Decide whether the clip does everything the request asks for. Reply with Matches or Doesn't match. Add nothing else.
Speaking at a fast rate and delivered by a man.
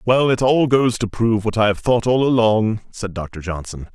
Matches